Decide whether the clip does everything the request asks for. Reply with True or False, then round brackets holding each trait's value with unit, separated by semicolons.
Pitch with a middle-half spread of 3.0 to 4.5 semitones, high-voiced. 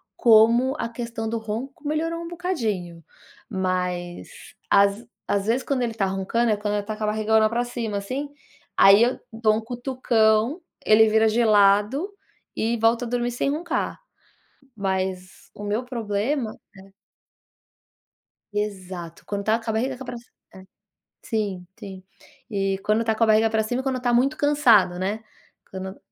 True (3.3 semitones; 220 Hz)